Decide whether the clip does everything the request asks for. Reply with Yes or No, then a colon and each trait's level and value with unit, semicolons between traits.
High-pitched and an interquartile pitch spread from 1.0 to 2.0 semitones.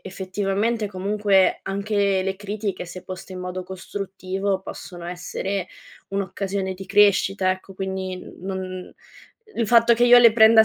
Yes: high, 195 Hz; narrow, 1.6 semitones